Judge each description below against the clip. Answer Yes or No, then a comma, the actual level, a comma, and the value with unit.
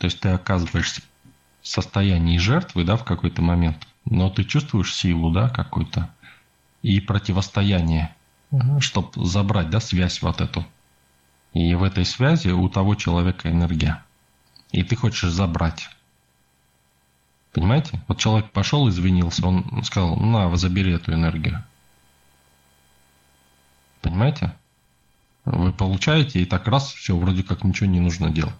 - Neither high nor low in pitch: No, very low, 90 Hz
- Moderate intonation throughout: No, wide, 6.9 semitones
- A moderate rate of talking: Yes, average, 130 wpm